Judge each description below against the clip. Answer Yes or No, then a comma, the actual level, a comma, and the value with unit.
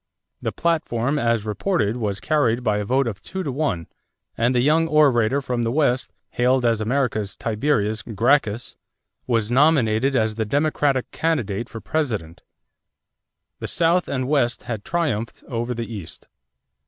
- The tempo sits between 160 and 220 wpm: No, average, 150 wpm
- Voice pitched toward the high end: No, low, 120 Hz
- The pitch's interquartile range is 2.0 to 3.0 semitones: No, average, 4.6 semitones